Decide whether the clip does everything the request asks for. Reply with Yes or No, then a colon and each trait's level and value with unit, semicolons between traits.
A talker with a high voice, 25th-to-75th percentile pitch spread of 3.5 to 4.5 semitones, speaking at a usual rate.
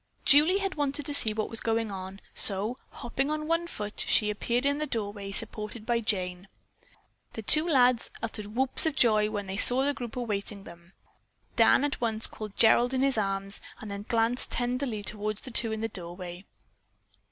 Yes: high, 225 Hz; average, 4.2 semitones; average, 185 wpm